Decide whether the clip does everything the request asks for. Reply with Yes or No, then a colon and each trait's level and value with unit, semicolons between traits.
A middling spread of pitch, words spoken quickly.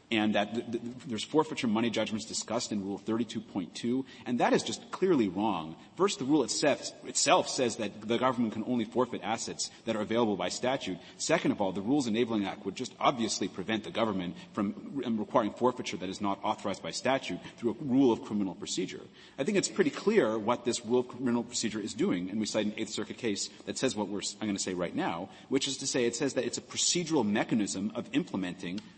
Yes: average, 3.0 semitones; fast, 225 wpm